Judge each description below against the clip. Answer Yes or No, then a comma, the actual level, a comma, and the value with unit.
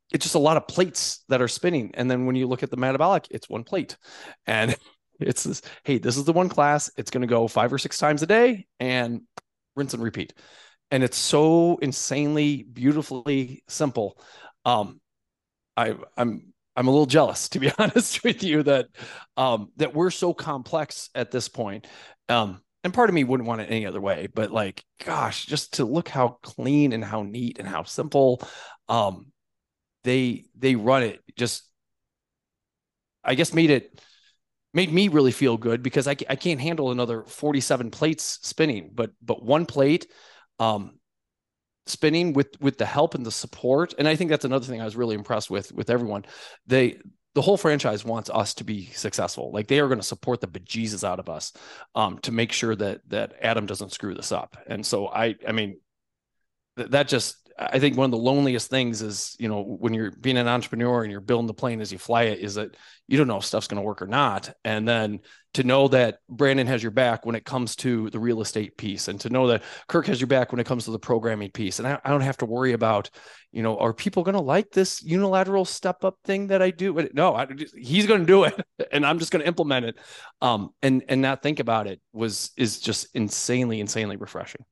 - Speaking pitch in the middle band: No, low, 130 Hz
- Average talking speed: No, fast, 215 wpm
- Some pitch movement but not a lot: Yes, average, 4.6 semitones